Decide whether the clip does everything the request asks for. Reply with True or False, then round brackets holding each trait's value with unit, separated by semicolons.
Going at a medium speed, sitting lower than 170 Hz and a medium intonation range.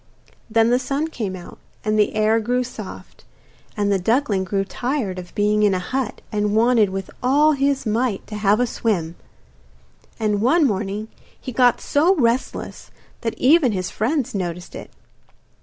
False (165 wpm; 220 Hz; 3.9 semitones)